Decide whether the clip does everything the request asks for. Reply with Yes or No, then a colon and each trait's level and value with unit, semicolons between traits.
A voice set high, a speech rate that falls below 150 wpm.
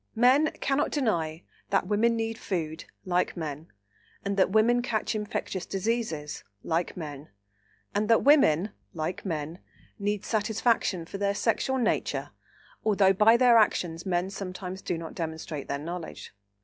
Yes: high, 195 Hz; average, 140 wpm